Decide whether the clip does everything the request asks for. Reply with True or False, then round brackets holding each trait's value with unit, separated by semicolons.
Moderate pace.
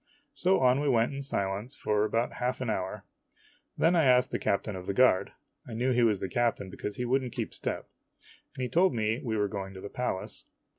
False (235 wpm)